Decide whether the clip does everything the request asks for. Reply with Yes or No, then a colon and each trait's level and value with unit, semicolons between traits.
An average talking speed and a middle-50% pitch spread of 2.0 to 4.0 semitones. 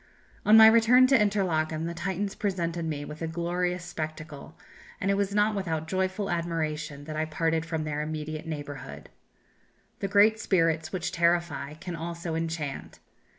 Yes: average, 155 wpm; average, 3.2 semitones